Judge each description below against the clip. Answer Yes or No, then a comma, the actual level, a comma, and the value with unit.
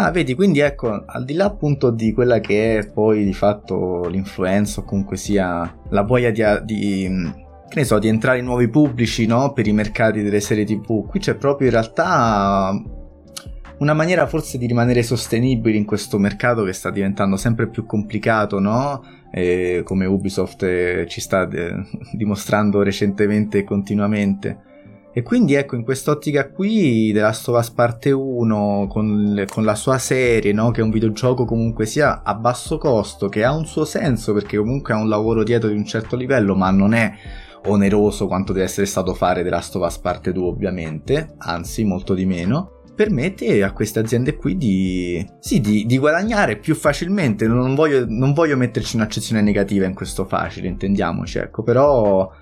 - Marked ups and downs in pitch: No, average, 3.7 semitones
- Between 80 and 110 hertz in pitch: Yes, low, 105 Hz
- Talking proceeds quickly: Yes, fast, 180 wpm